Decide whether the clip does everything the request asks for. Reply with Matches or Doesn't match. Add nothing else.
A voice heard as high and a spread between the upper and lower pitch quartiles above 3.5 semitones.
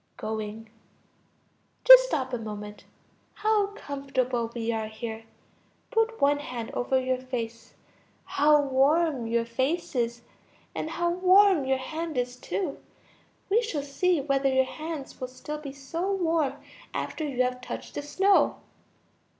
Matches